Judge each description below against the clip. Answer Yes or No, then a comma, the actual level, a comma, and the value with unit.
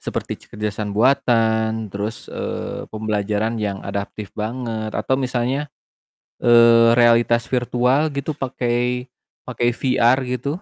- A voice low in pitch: Yes, low, 120 Hz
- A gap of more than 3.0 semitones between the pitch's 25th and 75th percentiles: No, narrow, 2.5 semitones